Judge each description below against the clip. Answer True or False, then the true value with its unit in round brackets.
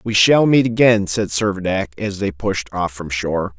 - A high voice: False (100 Hz)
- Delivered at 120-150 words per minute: False (200 wpm)